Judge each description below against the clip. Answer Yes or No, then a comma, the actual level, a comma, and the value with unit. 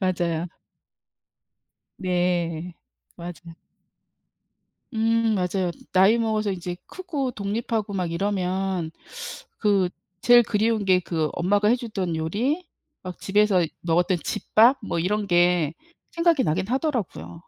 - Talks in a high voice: Yes, high, 195 Hz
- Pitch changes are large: No, average, 4.0 semitones